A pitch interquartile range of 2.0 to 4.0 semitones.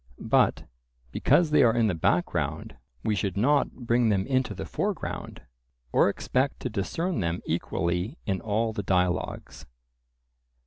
No: wide, 5.5 semitones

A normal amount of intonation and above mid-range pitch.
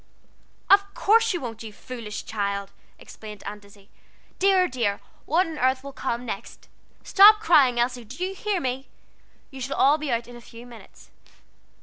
No: wide, 7.4 semitones; very high, 255 Hz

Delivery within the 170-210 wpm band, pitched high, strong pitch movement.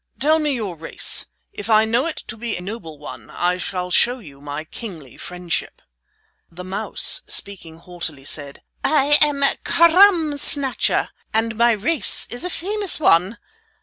No: average, 155 wpm; high, 215 Hz; wide, 8.8 semitones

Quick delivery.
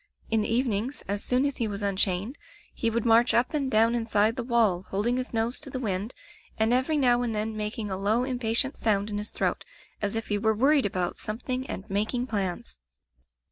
Yes: fast, 220 wpm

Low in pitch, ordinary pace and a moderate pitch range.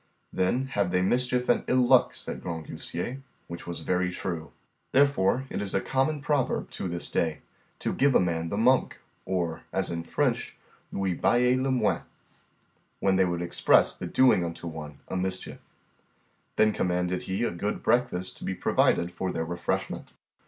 No: very low, 95 Hz; average, 170 wpm; wide, 6.1 semitones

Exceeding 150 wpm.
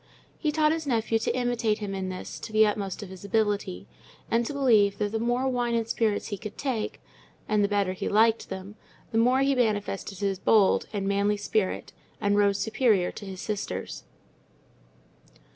Yes: average, 185 wpm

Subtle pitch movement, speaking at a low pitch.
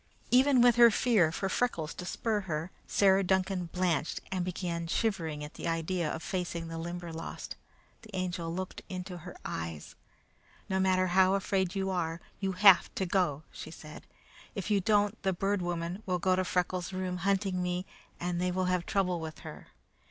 No: narrow, 2.1 semitones; medium, 180 Hz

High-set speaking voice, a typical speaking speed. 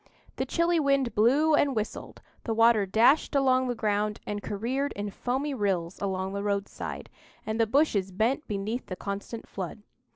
Yes: high, 220 Hz; average, 165 wpm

